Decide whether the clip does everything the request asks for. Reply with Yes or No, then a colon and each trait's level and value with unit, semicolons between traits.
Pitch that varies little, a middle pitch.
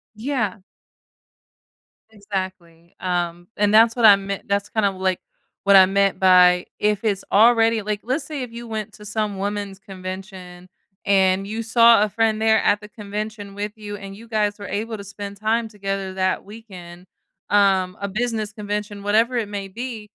No: narrow, 2.2 semitones; high, 205 Hz